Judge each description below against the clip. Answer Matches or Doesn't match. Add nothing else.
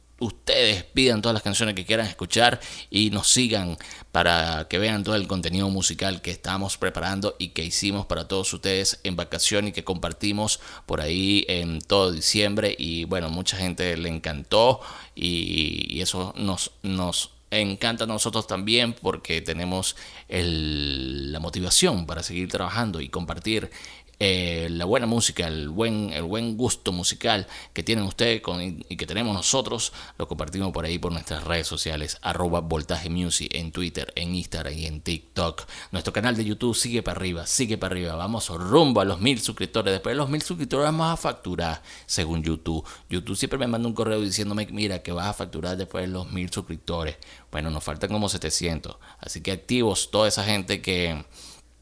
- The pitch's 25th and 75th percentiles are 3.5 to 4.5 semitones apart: Matches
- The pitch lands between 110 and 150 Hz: Doesn't match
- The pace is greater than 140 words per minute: Matches